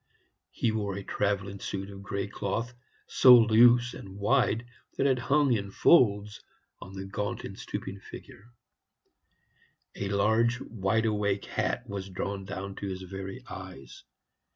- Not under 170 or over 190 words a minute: No, average, 145 wpm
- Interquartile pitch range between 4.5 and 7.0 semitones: No, narrow, 2.5 semitones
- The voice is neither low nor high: No, low, 100 Hz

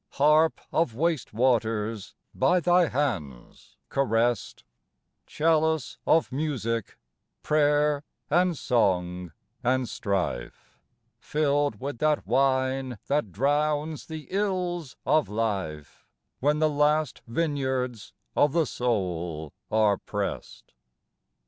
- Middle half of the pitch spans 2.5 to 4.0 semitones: No, wide, 5.4 semitones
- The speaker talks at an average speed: No, slow, 100 wpm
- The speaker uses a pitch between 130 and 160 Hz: Yes, low, 135 Hz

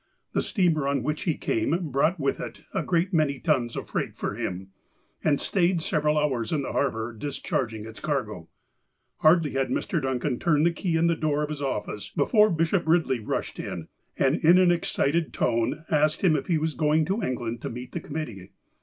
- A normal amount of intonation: Yes, average, 4.4 semitones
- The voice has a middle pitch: Yes, medium, 150 Hz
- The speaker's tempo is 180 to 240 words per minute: Yes, fast, 205 wpm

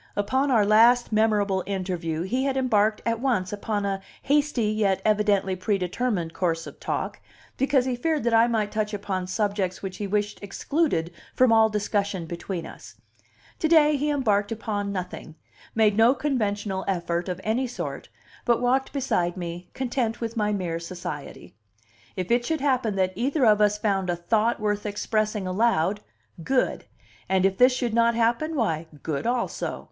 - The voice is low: No, high, 210 Hz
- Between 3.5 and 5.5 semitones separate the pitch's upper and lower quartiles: Yes, average, 4.1 semitones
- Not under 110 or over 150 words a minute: No, average, 165 wpm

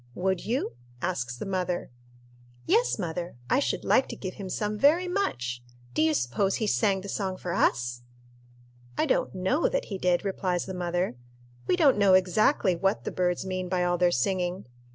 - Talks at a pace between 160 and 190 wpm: Yes, average, 185 wpm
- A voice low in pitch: No, medium, 185 Hz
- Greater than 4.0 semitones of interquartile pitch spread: No, average, 2.7 semitones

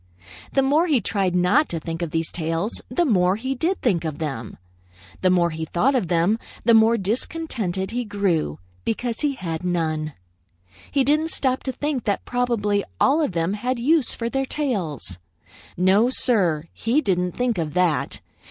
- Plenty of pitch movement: Yes, wide, 6.9 semitones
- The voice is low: No, high, 205 Hz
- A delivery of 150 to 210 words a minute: Yes, average, 175 wpm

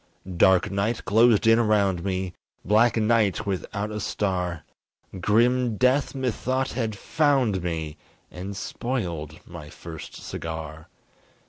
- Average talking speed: No, slow, 115 wpm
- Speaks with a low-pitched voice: Yes, low, 105 Hz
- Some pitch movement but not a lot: Yes, average, 4.7 semitones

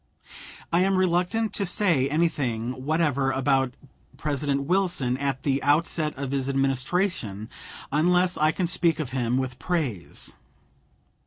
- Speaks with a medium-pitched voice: Yes, medium, 145 Hz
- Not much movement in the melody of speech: No, average, 4.7 semitones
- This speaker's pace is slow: Yes, slow, 130 wpm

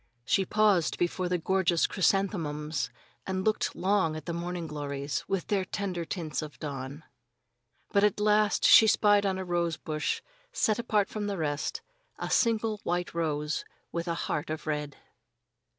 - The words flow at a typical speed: Yes, average, 160 wpm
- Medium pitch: Yes, medium, 175 Hz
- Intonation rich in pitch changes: No, average, 4.5 semitones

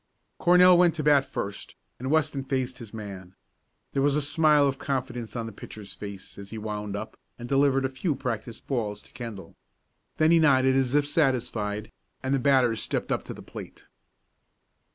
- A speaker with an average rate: Yes, average, 190 wpm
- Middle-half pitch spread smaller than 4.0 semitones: No, average, 4.7 semitones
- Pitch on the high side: No, low, 130 Hz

